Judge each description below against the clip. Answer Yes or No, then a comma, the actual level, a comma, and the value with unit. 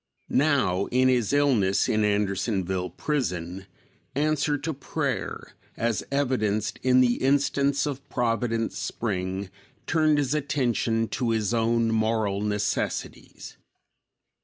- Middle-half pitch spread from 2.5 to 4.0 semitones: No, average, 5.0 semitones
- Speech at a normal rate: No, slow, 110 wpm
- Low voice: Yes, low, 115 Hz